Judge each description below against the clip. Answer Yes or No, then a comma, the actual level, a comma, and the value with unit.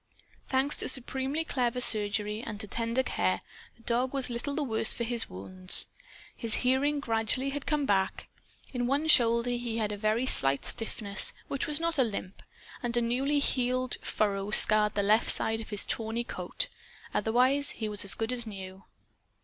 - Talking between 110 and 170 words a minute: No, average, 180 wpm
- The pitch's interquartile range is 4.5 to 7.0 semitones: No, average, 3.5 semitones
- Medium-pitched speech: No, high, 235 Hz